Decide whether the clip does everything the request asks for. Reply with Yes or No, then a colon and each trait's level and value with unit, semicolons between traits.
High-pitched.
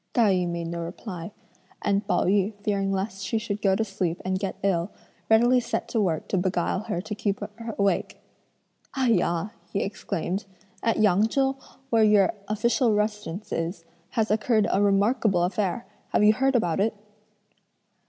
Yes: high, 200 Hz